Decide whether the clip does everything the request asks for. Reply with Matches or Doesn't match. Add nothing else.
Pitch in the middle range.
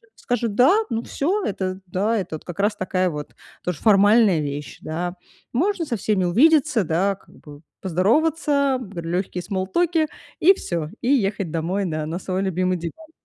Doesn't match